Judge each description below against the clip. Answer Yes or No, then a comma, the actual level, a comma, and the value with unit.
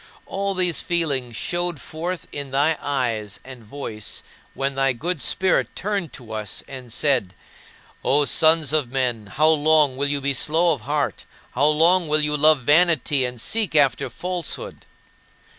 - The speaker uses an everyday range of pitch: Yes, average, 3.9 semitones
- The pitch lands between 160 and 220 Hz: No, medium, 145 Hz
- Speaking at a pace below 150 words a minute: No, average, 160 wpm